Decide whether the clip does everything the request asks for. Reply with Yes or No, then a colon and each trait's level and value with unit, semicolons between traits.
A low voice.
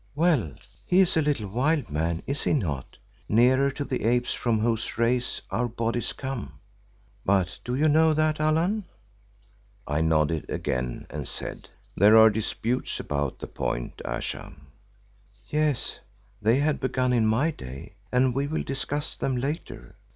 Yes: low, 125 Hz